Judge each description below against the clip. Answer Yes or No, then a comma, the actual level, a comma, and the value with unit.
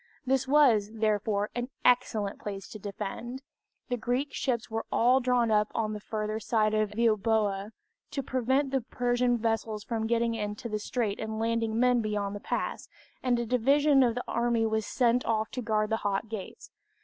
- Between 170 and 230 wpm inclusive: Yes, average, 180 wpm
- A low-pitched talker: No, high, 225 Hz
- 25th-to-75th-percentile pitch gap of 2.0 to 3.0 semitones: Yes, narrow, 2.5 semitones